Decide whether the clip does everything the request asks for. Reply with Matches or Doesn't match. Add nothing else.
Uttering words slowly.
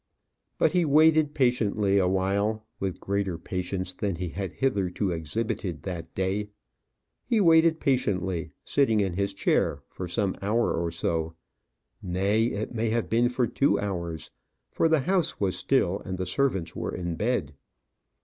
Doesn't match